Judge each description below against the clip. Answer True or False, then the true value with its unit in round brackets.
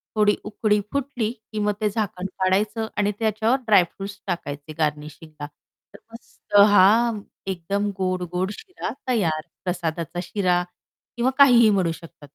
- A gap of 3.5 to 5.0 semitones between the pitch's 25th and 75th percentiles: True (3.8 semitones)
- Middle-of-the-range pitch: False (200 Hz)